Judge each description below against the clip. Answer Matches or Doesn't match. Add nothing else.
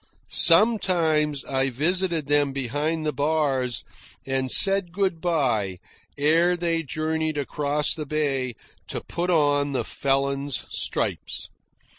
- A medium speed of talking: Doesn't match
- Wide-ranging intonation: Doesn't match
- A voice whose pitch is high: Doesn't match